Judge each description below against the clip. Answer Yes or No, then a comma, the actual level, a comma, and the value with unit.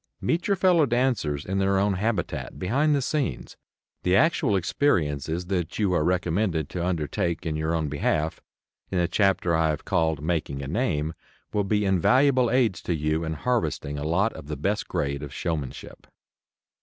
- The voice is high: No, very low, 90 Hz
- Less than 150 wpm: No, average, 175 wpm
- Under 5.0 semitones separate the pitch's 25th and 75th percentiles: No, wide, 5.4 semitones